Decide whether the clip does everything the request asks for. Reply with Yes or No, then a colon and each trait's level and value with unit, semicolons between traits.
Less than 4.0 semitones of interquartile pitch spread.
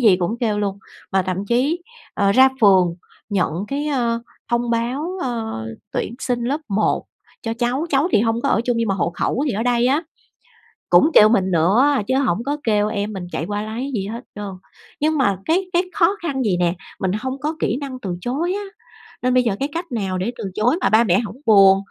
No: average, 5.3 semitones